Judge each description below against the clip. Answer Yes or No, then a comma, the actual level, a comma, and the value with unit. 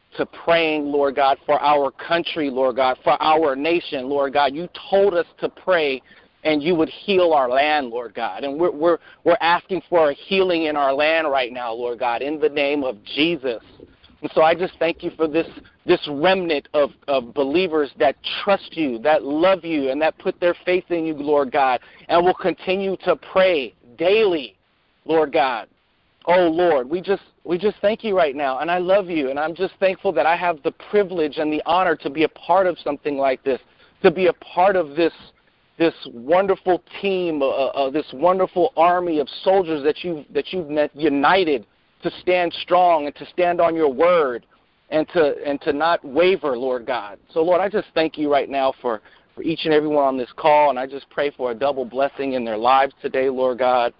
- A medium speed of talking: No, fast, 210 wpm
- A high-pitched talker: No, medium, 160 Hz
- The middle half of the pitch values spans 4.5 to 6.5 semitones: No, average, 3.8 semitones